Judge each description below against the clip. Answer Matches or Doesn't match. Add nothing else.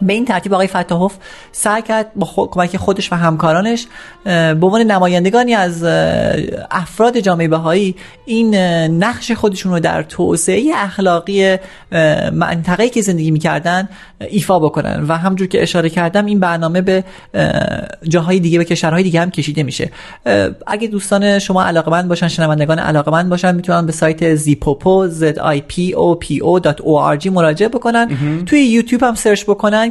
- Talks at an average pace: Matches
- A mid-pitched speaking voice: Matches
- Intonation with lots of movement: Doesn't match